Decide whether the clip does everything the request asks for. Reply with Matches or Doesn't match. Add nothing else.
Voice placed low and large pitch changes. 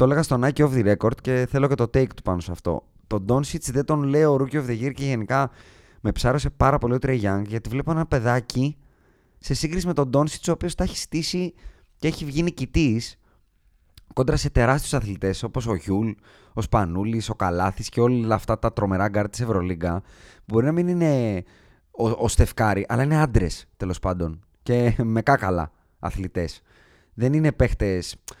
Matches